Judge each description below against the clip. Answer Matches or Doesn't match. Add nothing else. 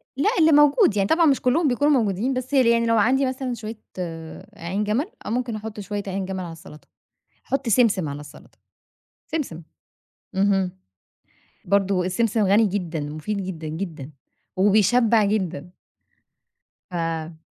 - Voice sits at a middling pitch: Doesn't match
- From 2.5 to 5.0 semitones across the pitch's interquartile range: Doesn't match